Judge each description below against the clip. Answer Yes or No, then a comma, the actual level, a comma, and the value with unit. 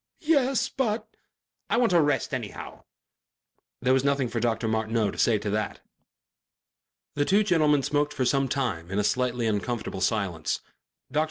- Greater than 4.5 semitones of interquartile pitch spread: Yes, average, 5.3 semitones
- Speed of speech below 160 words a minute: No, average, 165 wpm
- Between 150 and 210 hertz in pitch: No, low, 130 Hz